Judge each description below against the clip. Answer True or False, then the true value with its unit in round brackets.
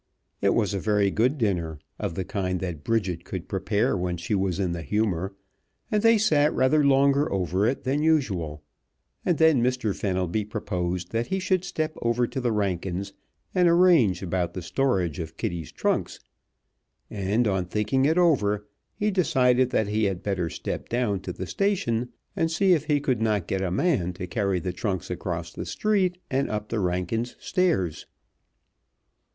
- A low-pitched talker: True (105 Hz)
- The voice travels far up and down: True (7.0 semitones)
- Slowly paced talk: False (175 wpm)